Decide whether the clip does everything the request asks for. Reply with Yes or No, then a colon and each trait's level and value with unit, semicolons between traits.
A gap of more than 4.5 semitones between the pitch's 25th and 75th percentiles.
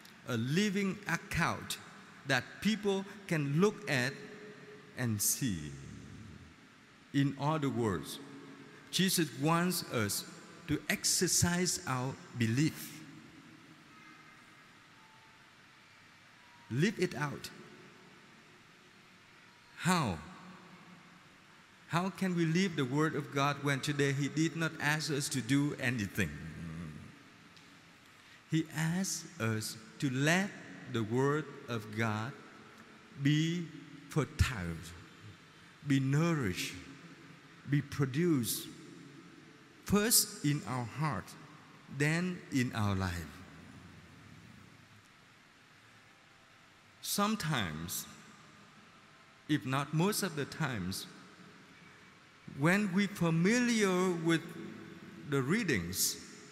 Yes: average, 5.2 semitones